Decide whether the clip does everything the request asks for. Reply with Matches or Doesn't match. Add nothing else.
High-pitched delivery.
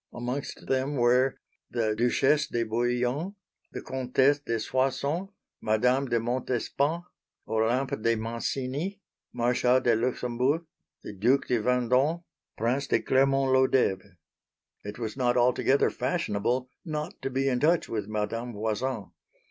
Doesn't match